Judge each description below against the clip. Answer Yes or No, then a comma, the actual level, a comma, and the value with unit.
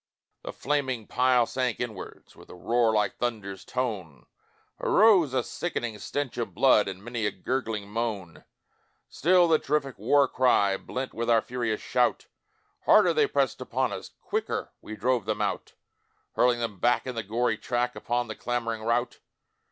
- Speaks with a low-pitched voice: Yes, low, 120 Hz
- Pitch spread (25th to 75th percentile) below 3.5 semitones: Yes, average, 3.0 semitones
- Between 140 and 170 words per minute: Yes, average, 160 wpm